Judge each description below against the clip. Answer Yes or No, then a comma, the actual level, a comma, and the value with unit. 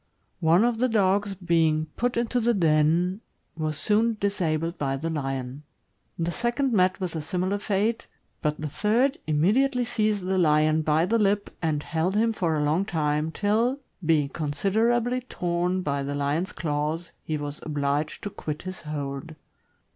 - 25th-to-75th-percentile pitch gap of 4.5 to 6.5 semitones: Yes, wide, 5.5 semitones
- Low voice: No, medium, 170 Hz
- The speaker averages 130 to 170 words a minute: Yes, average, 165 wpm